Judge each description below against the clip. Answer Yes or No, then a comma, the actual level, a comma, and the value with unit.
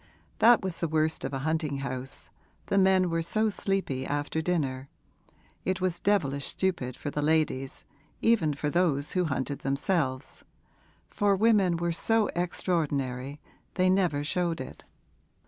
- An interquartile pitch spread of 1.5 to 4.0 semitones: No, average, 4.8 semitones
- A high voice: No, medium, 160 Hz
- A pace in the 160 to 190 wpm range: No, average, 145 wpm